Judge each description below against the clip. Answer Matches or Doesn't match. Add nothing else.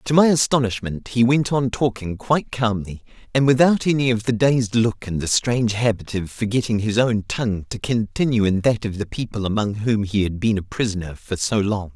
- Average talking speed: Doesn't match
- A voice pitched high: Doesn't match